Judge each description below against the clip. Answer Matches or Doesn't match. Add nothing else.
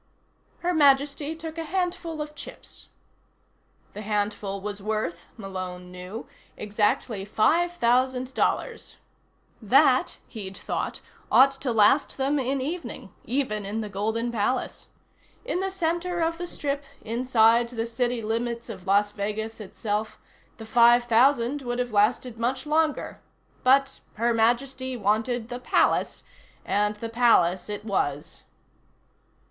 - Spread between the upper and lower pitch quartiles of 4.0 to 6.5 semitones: Matches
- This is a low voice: Doesn't match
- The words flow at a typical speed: Doesn't match